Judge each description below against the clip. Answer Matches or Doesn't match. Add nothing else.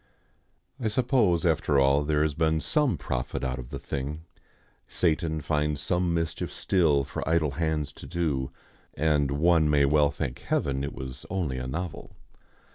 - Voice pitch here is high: Doesn't match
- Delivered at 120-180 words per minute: Matches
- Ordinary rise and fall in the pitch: Matches